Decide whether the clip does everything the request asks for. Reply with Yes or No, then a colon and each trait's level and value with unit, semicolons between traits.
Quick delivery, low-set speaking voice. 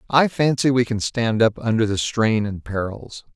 No: average, 195 wpm; low, 115 Hz